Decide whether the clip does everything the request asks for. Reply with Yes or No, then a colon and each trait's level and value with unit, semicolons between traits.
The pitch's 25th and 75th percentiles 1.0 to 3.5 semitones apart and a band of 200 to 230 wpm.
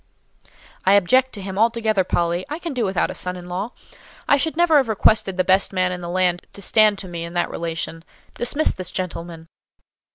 No: average, 4.3 semitones; fast, 205 wpm